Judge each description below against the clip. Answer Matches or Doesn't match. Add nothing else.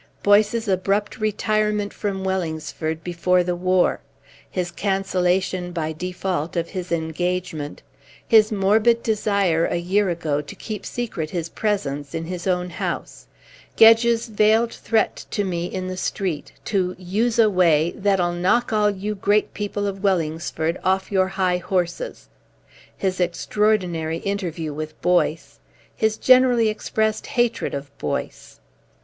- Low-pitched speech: Doesn't match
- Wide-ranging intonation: Doesn't match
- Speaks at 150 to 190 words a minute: Doesn't match